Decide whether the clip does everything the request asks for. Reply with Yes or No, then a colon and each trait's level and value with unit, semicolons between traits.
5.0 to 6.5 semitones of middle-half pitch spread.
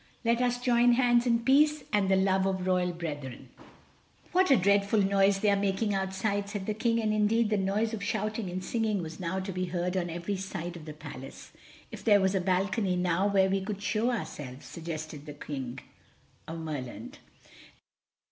No: average, 3.5 semitones